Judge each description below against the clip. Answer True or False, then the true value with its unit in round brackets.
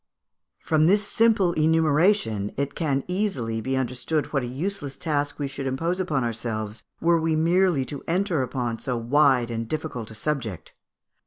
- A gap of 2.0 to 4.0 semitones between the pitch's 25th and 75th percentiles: False (5.2 semitones)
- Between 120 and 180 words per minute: True (160 wpm)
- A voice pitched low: False (145 Hz)